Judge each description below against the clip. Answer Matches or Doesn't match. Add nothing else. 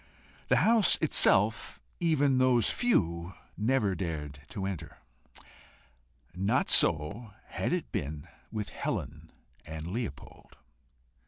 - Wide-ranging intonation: Matches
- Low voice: Matches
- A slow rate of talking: Matches